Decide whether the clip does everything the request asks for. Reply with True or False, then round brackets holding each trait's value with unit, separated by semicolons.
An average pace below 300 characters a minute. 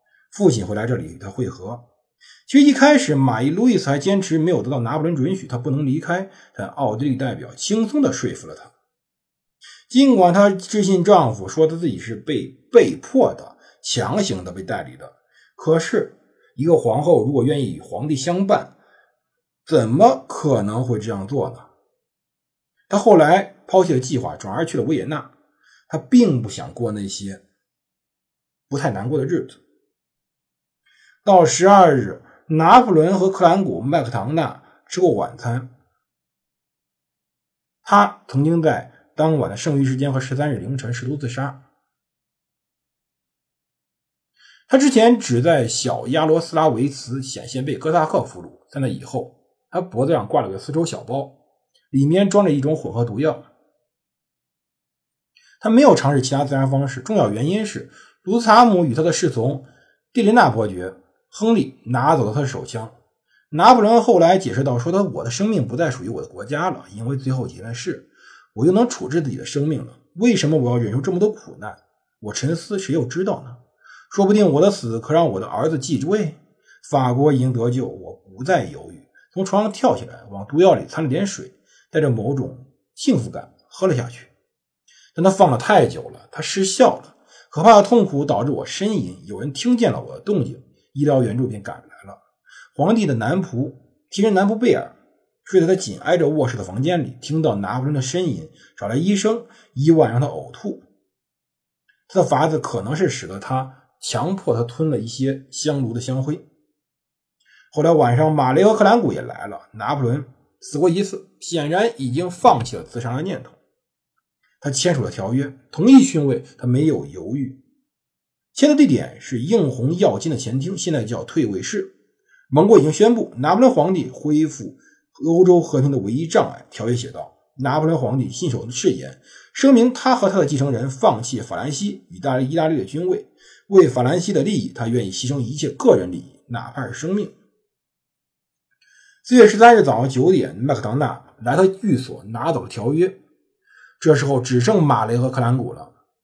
True (265 characters per minute)